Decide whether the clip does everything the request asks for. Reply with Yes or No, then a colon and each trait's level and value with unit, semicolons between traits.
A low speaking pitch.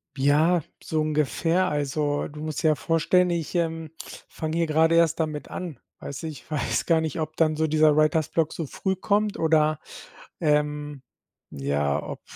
No: medium, 155 Hz